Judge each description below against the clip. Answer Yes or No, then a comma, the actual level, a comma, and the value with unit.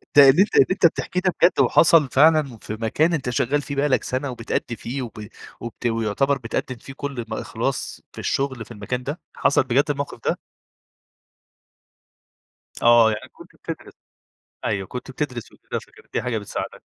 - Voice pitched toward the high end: No, low, 130 Hz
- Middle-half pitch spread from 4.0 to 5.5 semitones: No, average, 3.6 semitones